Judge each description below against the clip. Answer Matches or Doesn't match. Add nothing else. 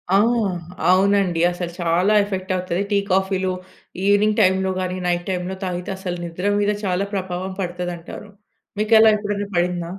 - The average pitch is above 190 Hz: Doesn't match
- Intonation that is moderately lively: Doesn't match